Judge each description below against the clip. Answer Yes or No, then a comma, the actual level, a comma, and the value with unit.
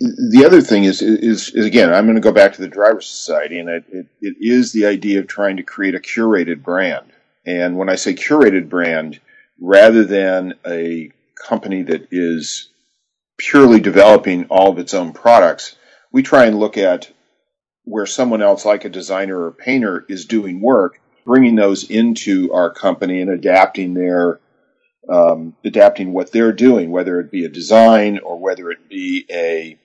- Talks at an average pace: Yes, average, 180 wpm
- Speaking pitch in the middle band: No, low, 100 Hz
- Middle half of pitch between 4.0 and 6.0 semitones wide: Yes, wide, 5.4 semitones